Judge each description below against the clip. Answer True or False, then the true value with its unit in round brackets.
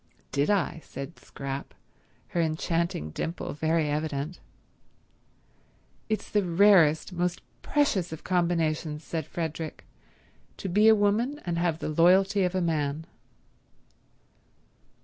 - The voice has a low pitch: False (170 Hz)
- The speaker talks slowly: True (115 wpm)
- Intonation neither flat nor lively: True (3.3 semitones)